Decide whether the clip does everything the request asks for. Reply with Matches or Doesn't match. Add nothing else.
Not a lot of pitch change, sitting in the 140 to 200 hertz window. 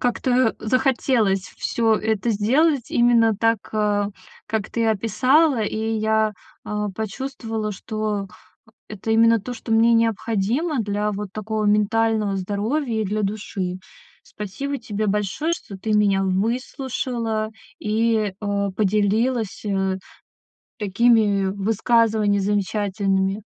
Doesn't match